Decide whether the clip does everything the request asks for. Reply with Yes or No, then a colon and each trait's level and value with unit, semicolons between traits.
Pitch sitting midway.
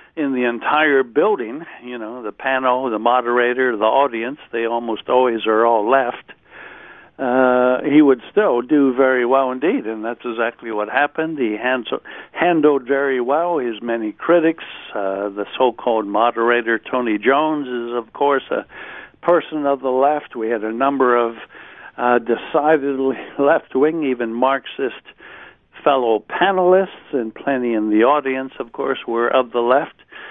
No: low, 125 Hz